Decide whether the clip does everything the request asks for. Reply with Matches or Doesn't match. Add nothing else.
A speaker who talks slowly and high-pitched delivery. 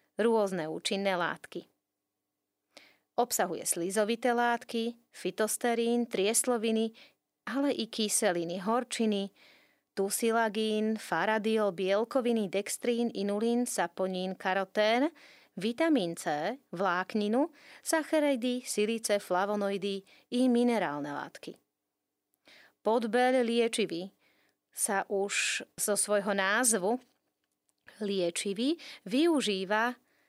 Matches